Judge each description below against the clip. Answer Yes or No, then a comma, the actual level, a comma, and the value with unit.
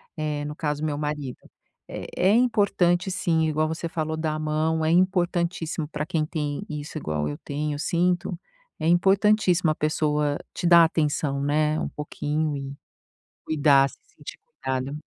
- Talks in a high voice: No, medium, 155 Hz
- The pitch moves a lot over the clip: No, narrow, 2.5 semitones